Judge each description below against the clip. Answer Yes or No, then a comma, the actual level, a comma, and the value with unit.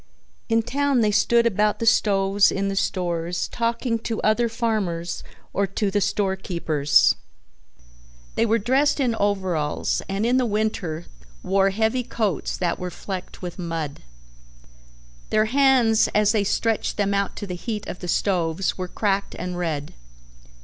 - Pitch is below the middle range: No, high, 200 Hz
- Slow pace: No, average, 155 wpm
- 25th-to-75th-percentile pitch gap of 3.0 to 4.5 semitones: Yes, average, 3.8 semitones